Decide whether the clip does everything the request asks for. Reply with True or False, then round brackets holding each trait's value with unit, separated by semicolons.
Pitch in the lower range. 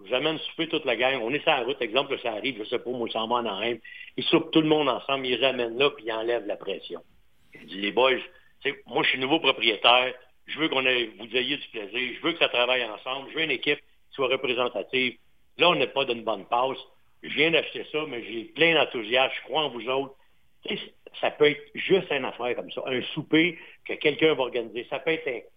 True (130 Hz)